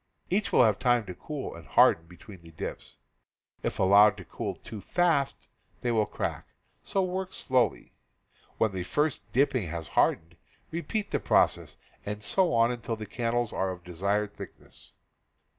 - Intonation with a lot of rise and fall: Yes, wide, 6.1 semitones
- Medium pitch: No, low, 110 Hz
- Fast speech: No, average, 170 wpm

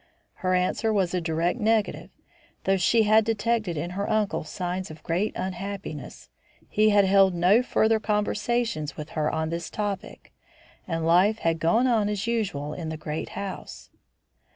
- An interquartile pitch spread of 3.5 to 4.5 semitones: Yes, average, 4.2 semitones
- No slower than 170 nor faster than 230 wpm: No, average, 160 wpm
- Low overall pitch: No, high, 195 Hz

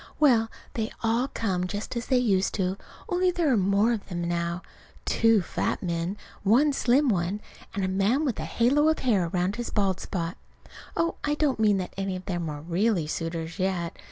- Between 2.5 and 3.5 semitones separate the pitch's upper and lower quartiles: No, average, 5.1 semitones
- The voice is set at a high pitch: Yes, high, 200 Hz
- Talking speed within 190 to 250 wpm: Yes, average, 195 wpm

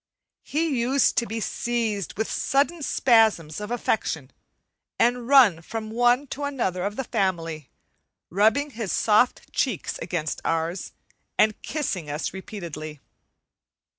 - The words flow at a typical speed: No, slow, 125 wpm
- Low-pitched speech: No, high, 220 Hz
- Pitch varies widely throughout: Yes, wide, 6.0 semitones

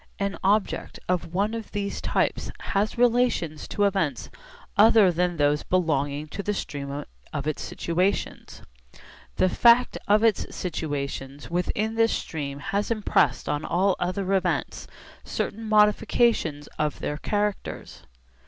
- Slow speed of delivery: Yes, slow, 130 wpm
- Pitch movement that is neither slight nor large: No, wide, 5.9 semitones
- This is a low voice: No, medium, 185 Hz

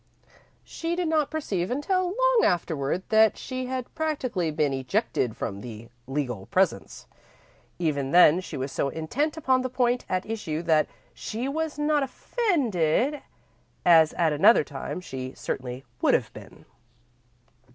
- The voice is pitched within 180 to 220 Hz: Yes, medium, 185 Hz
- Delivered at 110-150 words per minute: Yes, average, 140 wpm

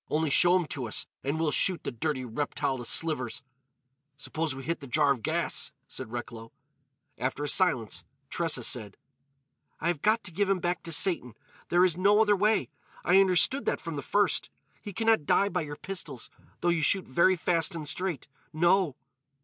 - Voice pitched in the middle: Yes, medium, 165 Hz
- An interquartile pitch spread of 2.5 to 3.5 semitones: No, average, 5.1 semitones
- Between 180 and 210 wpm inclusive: Yes, average, 190 wpm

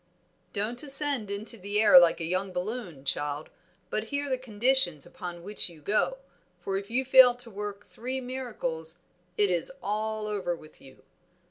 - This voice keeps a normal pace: Yes, average, 165 wpm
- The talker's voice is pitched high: Yes, high, 210 Hz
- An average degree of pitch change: No, wide, 5.8 semitones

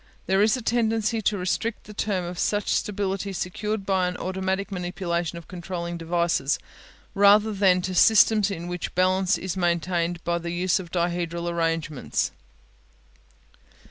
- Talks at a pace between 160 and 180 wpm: No, average, 140 wpm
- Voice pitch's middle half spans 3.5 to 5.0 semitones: No, average, 2.7 semitones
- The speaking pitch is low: No, medium, 185 Hz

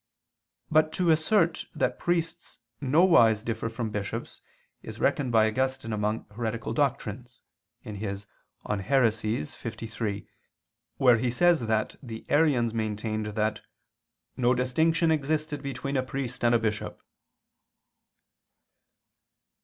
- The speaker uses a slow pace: Yes, slow, 110 wpm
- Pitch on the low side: Yes, low, 120 Hz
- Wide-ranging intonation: No, average, 4.9 semitones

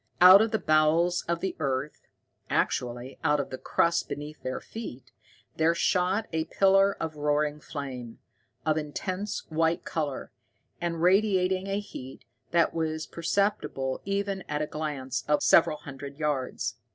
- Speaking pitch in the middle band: Yes, medium, 160 Hz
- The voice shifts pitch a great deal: No, average, 4.2 semitones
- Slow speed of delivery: No, average, 145 wpm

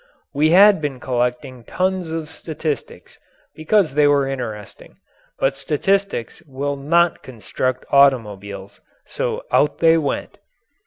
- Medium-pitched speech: Yes, medium, 145 Hz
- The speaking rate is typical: No, slow, 115 wpm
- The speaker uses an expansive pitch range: No, average, 4.3 semitones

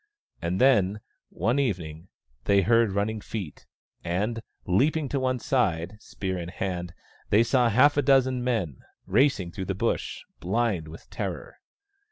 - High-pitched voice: No, low, 105 Hz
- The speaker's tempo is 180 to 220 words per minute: No, average, 145 wpm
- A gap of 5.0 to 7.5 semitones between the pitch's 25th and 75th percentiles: Yes, wide, 5.6 semitones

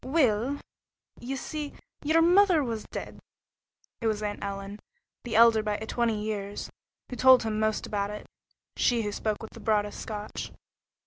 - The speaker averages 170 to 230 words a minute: No, average, 155 wpm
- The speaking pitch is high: Yes, high, 220 Hz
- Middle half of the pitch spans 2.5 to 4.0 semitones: Yes, average, 3.6 semitones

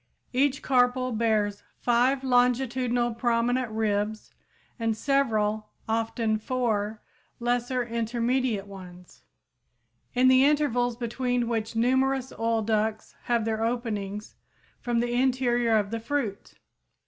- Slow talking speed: Yes, slow, 110 wpm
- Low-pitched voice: No, high, 235 Hz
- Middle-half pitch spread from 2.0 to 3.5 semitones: Yes, narrow, 2.4 semitones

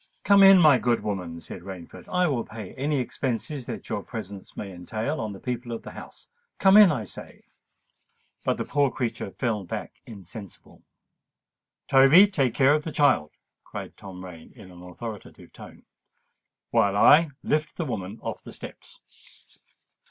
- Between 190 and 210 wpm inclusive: No, average, 160 wpm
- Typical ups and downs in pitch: No, wide, 7.2 semitones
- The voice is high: No, low, 120 Hz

